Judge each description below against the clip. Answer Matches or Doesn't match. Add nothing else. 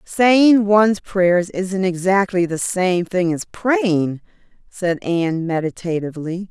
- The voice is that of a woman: Matches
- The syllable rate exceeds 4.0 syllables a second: Doesn't match